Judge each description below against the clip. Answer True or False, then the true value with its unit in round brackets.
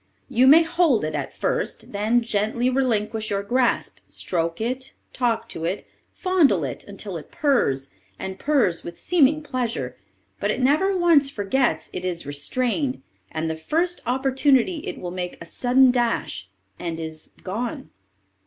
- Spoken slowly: False (155 wpm)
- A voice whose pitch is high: True (235 Hz)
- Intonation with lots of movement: True (6.9 semitones)